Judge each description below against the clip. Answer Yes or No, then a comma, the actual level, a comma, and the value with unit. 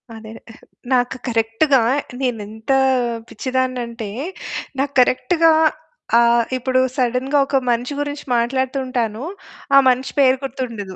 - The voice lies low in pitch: No, very high, 250 Hz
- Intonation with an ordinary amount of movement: No, narrow, 2.2 semitones